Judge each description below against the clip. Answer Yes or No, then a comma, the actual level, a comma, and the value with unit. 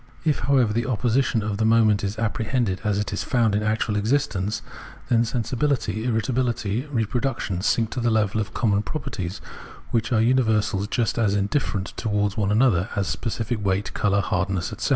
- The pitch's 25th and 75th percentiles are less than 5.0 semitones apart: Yes, average, 2.8 semitones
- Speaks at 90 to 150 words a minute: No, average, 175 wpm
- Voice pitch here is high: No, low, 110 Hz